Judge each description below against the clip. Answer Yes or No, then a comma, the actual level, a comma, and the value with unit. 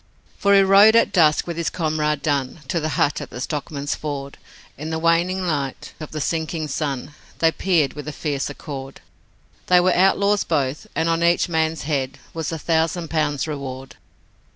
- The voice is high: No, medium, 155 Hz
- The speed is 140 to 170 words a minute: No, average, 180 wpm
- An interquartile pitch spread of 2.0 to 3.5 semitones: Yes, average, 2.8 semitones